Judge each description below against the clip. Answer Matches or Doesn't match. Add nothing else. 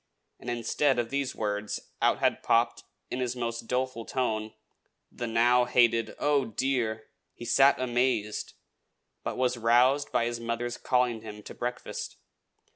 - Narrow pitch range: Matches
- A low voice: Matches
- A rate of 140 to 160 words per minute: Matches